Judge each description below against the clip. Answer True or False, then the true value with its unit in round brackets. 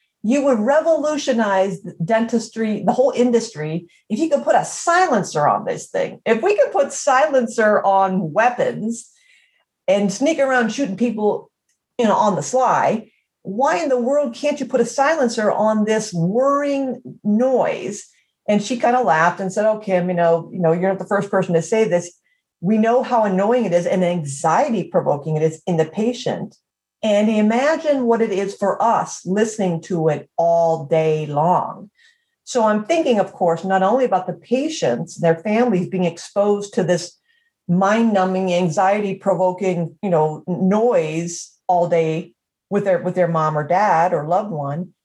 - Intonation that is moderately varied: False (5.9 semitones)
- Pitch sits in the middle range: False (205 Hz)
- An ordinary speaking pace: True (175 wpm)